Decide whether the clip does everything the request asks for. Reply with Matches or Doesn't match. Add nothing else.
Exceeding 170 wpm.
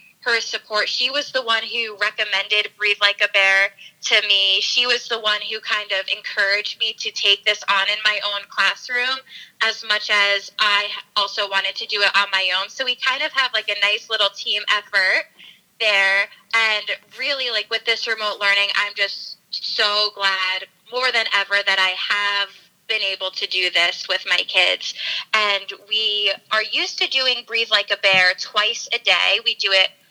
Matches